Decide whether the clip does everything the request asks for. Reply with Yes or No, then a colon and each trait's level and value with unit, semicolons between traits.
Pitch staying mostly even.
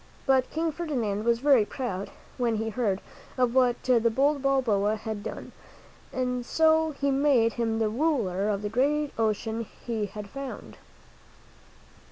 No: average, 4.0 semitones